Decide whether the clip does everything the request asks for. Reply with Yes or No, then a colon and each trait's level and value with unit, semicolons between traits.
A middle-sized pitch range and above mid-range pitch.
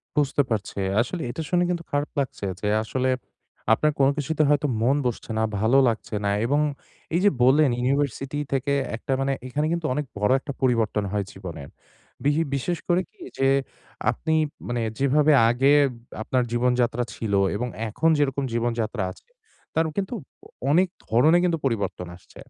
No: average, 4.3 semitones; low, 135 Hz